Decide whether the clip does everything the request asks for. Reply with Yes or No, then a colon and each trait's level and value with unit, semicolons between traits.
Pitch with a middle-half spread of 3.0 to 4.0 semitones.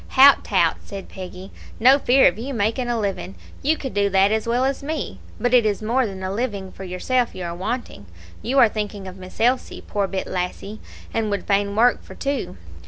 No: average, 4.4 semitones